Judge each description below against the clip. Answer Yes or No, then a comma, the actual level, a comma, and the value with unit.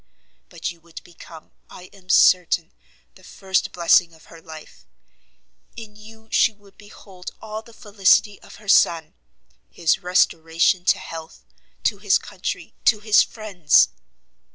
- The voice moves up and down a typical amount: Yes, average, 3.9 semitones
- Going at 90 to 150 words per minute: Yes, average, 140 wpm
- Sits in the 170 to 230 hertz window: Yes, medium, 185 Hz